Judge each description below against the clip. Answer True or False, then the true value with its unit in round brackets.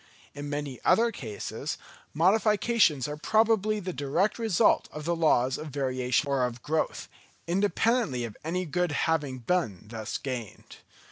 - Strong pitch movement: True (6.7 semitones)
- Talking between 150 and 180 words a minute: False (140 wpm)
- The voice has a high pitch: False (150 Hz)